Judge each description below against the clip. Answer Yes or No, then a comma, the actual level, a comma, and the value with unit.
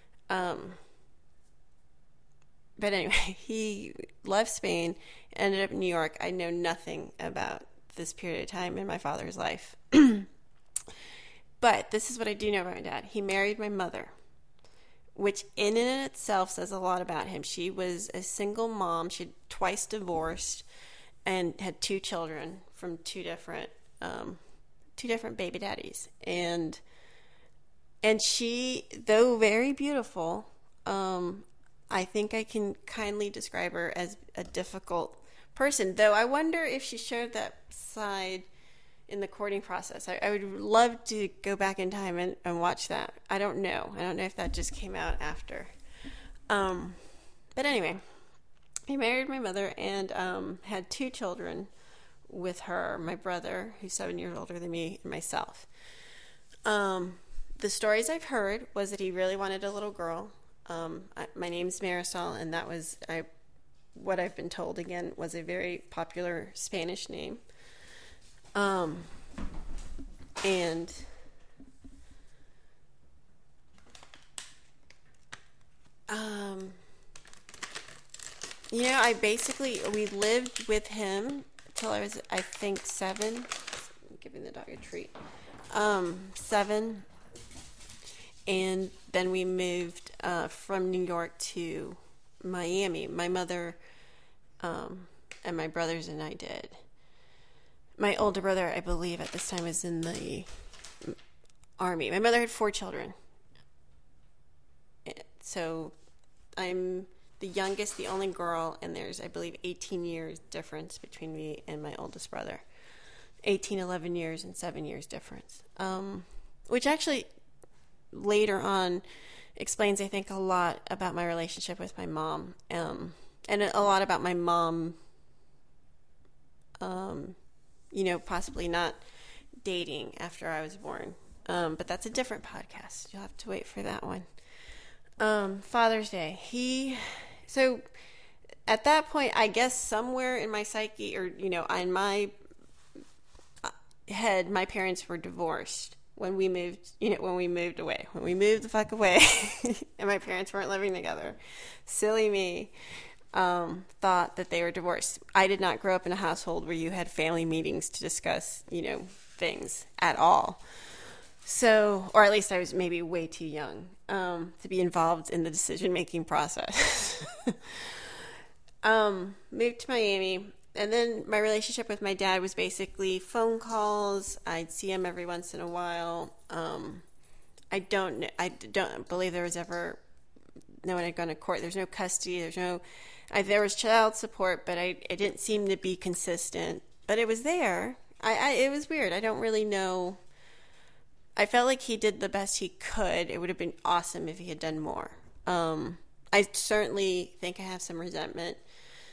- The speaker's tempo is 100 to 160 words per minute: Yes, average, 150 wpm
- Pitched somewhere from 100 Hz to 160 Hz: No, high, 190 Hz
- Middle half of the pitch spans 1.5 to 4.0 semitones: Yes, average, 3.4 semitones